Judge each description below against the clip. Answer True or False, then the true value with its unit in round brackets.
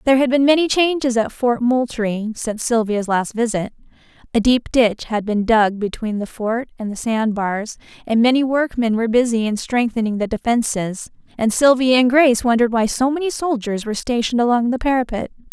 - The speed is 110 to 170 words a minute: False (185 wpm)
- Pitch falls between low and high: False (235 Hz)